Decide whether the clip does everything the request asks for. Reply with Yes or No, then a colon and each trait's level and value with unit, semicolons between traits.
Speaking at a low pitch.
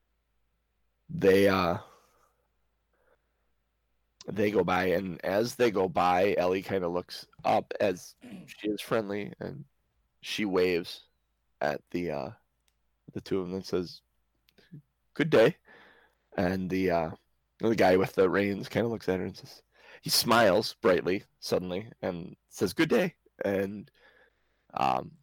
Yes: very low, 90 Hz